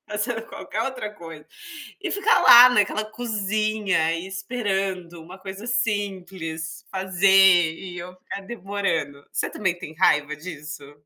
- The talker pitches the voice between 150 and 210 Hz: Yes, high, 190 Hz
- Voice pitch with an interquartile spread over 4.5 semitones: No, average, 4.2 semitones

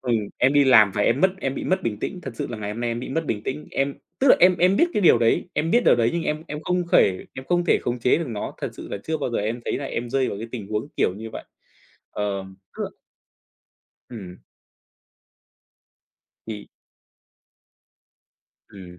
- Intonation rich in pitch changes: Yes, wide, 6.8 semitones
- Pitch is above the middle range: No, low, 125 Hz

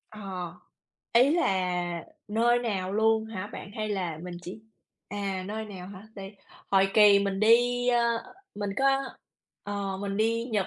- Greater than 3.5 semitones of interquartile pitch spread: No, average, 2.9 semitones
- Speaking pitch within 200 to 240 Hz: Yes, high, 205 Hz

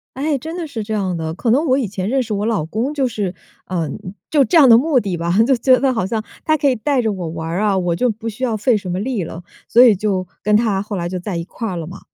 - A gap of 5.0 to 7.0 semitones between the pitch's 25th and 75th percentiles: Yes, wide, 5.6 semitones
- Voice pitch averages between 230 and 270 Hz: No, high, 215 Hz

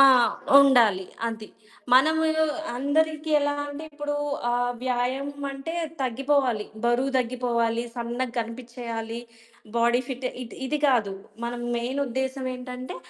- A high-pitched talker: Yes, very high, 255 Hz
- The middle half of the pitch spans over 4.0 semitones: No, average, 2.8 semitones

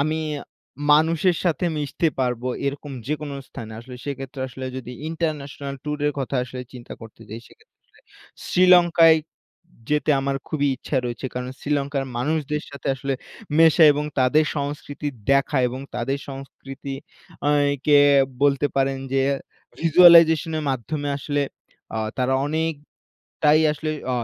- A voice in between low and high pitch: Yes, medium, 145 Hz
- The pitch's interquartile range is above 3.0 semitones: No, narrow, 2.5 semitones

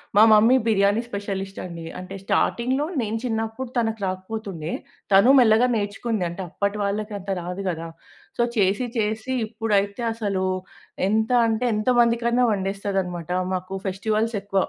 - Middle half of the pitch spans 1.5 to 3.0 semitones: Yes, narrow, 2.6 semitones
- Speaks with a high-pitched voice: Yes, high, 210 Hz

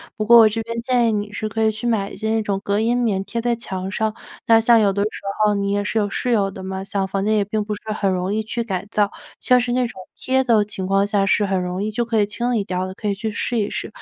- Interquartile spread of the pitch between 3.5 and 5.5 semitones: No, narrow, 2.4 semitones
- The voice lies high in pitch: Yes, high, 210 Hz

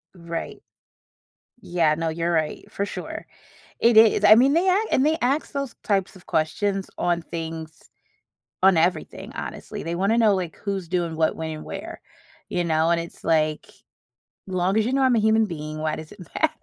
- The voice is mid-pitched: Yes, medium, 175 Hz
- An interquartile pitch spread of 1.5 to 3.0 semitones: No, average, 5.2 semitones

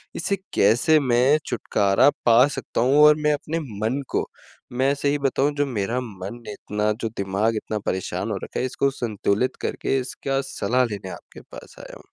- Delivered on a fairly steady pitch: No, average, 4.6 semitones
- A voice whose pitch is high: No, low, 125 Hz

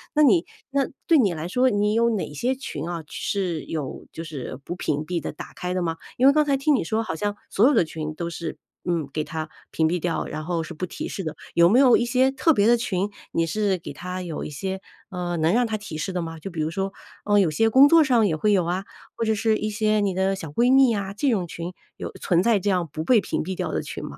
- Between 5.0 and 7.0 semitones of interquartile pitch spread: Yes, average, 5.3 semitones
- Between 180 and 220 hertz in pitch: Yes, high, 190 Hz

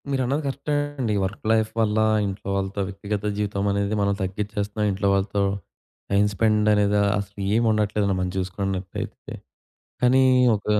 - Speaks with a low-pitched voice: Yes, low, 105 Hz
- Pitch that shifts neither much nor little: No, narrow, 1.5 semitones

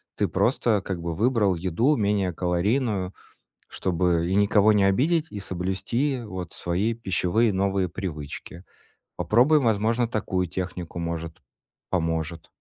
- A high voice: No, very low, 95 Hz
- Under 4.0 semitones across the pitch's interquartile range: No, average, 4.3 semitones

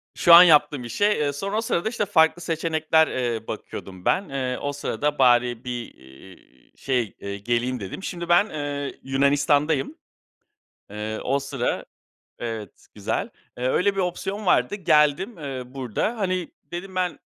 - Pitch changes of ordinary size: No, wide, 5.9 semitones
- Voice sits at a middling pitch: Yes, medium, 145 Hz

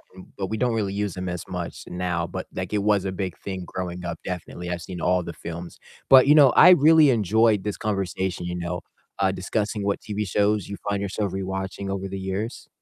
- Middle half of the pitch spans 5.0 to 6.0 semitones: No, narrow, 2.6 semitones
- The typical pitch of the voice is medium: No, very low, 95 Hz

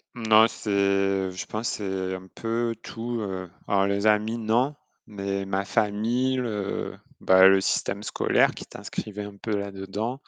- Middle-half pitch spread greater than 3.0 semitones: No, narrow, 2.5 semitones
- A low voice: Yes, low, 105 Hz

